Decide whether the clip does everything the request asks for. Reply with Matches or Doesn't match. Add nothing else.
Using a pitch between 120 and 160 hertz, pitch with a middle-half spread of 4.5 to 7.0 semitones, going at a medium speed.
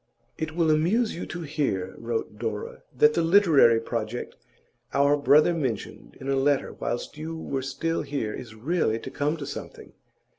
Matches